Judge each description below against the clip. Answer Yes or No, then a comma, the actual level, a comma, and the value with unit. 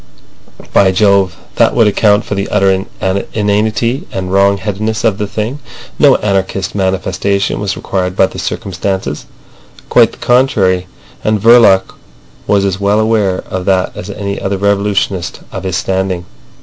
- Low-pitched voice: Yes, low, 100 Hz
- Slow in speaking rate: No, average, 150 wpm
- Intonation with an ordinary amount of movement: No, narrow, 1.7 semitones